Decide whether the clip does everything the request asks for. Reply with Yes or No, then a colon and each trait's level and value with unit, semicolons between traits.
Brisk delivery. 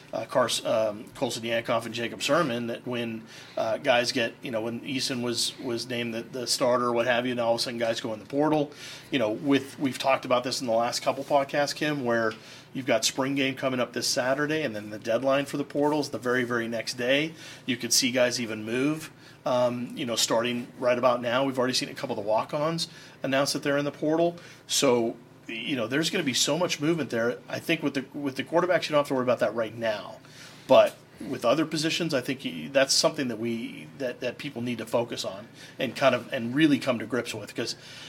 Yes: fast, 240 wpm